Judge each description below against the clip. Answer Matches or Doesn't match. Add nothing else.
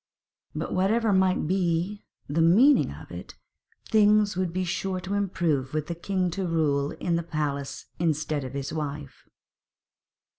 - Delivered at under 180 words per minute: Matches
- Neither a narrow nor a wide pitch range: Matches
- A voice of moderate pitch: Matches